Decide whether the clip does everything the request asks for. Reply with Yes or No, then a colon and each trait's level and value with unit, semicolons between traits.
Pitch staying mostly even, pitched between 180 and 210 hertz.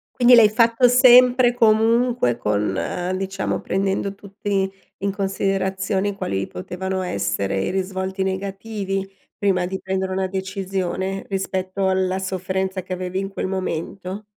Yes: narrow, 1.2 semitones; high, 190 Hz